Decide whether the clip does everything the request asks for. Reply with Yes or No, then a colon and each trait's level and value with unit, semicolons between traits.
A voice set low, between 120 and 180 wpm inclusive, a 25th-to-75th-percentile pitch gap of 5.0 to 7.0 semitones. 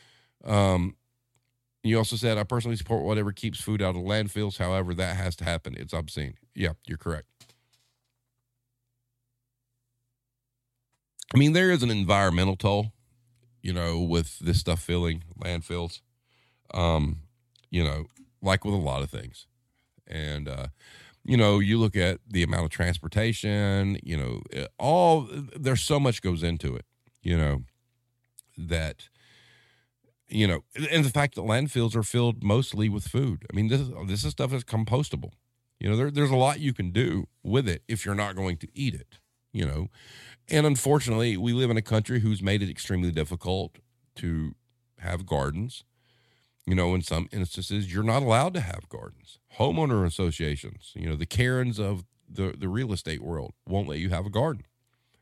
Yes: low, 110 Hz; average, 170 wpm; average, 5.3 semitones